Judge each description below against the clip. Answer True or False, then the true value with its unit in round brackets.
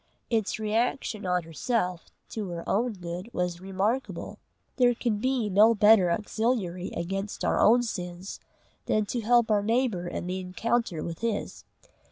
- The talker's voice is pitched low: False (205 Hz)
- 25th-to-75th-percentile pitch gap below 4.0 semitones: False (4.3 semitones)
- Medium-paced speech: True (150 wpm)